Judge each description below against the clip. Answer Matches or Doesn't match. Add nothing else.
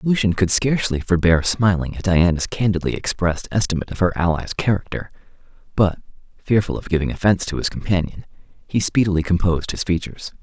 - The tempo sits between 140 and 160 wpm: Matches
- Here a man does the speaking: Matches